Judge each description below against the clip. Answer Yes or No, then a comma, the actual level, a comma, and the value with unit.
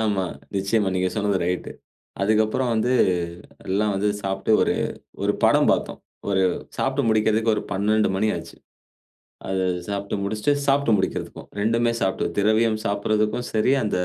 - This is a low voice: Yes, low, 105 Hz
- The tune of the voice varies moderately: No, narrow, 2.1 semitones